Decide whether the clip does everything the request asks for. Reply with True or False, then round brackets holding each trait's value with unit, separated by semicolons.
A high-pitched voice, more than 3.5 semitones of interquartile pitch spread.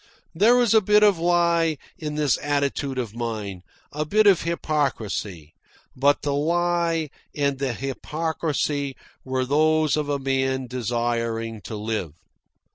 False (145 Hz; 5.1 semitones)